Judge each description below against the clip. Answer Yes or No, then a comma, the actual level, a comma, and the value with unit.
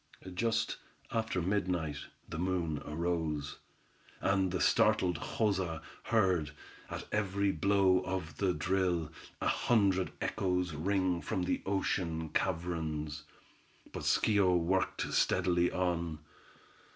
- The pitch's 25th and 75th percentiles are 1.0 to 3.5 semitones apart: Yes, average, 2.8 semitones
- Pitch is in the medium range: No, very low, 90 Hz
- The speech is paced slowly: Yes, slow, 110 wpm